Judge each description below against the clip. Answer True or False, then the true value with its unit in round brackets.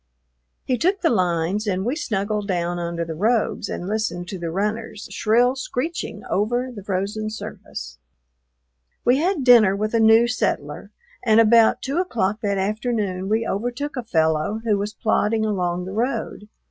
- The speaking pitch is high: True (215 Hz)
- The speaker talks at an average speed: True (160 wpm)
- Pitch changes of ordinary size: True (3.9 semitones)